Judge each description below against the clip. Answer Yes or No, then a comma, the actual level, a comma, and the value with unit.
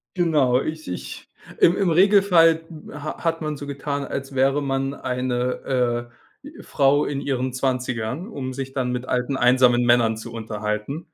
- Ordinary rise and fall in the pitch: Yes, average, 3.3 semitones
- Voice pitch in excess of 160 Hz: No, low, 135 Hz